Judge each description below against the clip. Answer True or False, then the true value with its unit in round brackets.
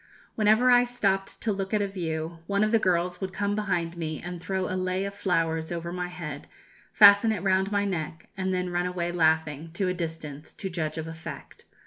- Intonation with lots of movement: False (3.2 semitones)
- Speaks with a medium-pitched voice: True (180 Hz)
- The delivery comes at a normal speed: False (210 wpm)